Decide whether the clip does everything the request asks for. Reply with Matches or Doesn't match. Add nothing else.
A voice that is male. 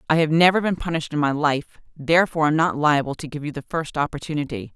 Doesn't match